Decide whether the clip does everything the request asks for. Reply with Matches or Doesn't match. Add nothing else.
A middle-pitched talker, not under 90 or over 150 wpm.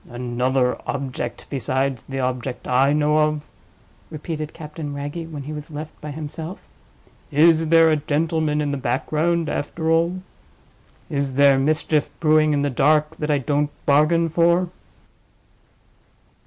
Matches